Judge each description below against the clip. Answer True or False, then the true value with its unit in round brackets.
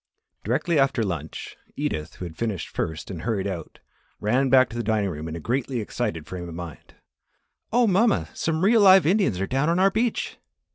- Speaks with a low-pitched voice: True (115 Hz)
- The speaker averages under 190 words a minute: False (195 wpm)